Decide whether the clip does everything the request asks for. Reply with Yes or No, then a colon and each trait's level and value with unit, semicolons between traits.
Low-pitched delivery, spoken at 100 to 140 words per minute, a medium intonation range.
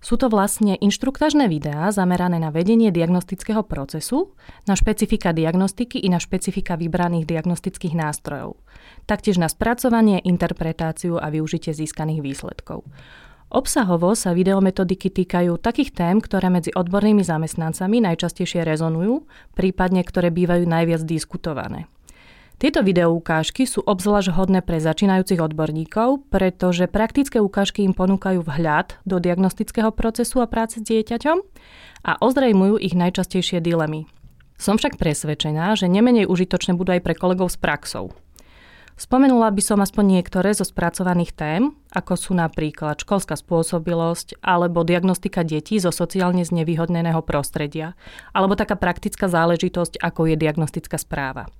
No: medium, 180 Hz; average, 130 wpm; average, 3.5 semitones